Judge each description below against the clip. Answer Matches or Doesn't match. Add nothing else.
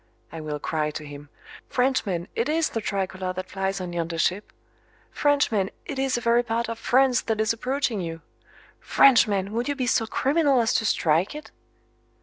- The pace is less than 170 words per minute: Doesn't match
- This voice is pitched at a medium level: Doesn't match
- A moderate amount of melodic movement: Doesn't match